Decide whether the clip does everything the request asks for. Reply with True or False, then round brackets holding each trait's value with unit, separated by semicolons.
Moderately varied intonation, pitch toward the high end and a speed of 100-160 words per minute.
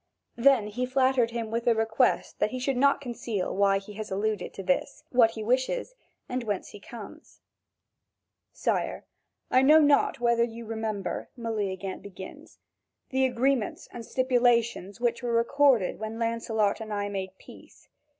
True (3.2 semitones; 230 Hz; 155 wpm)